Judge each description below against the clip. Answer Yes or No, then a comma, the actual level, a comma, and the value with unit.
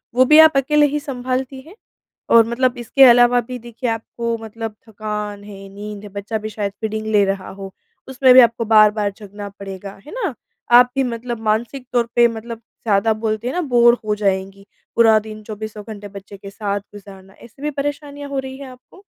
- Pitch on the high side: Yes, high, 225 Hz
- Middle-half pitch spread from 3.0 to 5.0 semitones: Yes, average, 3.6 semitones